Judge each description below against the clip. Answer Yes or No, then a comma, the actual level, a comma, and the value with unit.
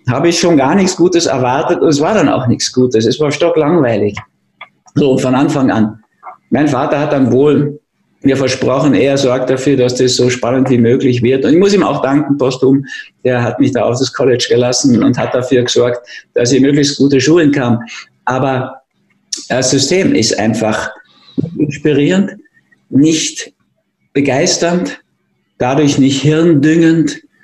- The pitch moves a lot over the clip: No, average, 3.6 semitones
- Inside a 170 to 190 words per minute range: No, average, 160 wpm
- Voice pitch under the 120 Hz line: No, low, 135 Hz